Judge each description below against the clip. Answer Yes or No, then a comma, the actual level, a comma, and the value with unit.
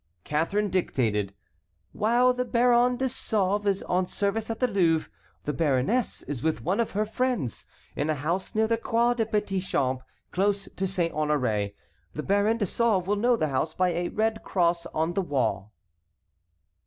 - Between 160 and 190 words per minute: Yes, average, 175 wpm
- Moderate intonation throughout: No, wide, 6.3 semitones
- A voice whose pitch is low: No, high, 190 Hz